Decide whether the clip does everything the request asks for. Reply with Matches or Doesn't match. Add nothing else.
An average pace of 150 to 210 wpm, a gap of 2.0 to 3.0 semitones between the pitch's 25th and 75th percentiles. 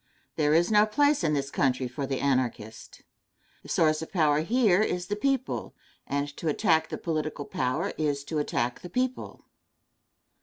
Doesn't match